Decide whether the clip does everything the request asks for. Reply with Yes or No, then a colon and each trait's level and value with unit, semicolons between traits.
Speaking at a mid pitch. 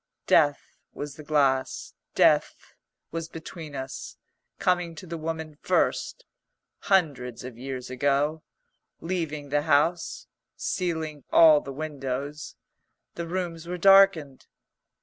Yes: medium, 155 Hz